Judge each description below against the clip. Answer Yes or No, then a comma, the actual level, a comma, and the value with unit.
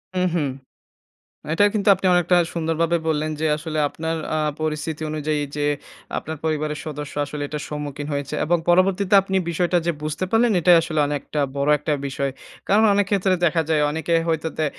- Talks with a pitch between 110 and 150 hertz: No, medium, 160 Hz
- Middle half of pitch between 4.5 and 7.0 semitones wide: No, average, 2.8 semitones